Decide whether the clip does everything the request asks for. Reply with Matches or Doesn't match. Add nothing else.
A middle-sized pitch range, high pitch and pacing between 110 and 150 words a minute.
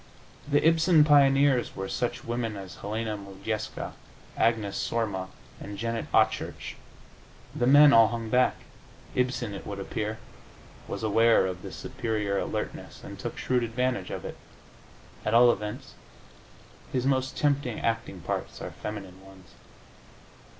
Doesn't match